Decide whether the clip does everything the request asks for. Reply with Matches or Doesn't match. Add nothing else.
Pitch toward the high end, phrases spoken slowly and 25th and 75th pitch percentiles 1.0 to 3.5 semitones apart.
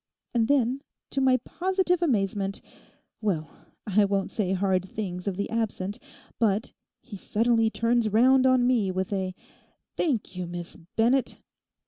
Doesn't match